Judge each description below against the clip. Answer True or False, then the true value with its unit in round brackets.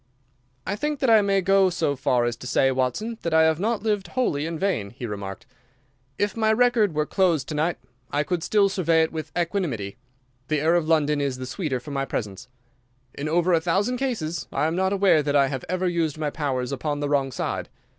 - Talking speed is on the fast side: True (220 wpm)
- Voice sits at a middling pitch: True (160 Hz)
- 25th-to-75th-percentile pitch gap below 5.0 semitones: False (5.5 semitones)